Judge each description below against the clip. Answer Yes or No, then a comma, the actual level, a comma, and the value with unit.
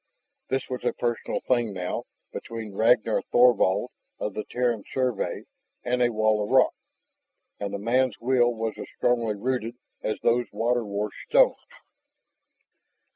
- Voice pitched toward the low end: Yes, low, 115 Hz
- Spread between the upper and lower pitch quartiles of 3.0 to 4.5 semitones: No, narrow, 2.6 semitones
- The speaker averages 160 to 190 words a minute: No, average, 140 wpm